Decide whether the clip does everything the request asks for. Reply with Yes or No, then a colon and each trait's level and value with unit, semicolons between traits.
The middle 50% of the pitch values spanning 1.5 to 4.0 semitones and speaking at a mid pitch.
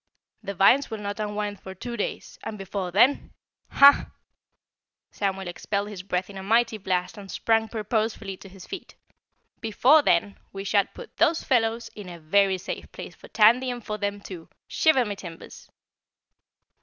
No: average, 2.8 semitones; high, 205 Hz